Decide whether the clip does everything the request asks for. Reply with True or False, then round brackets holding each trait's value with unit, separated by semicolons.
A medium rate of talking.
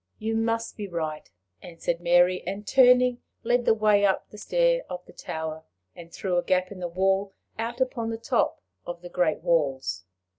True (185 wpm)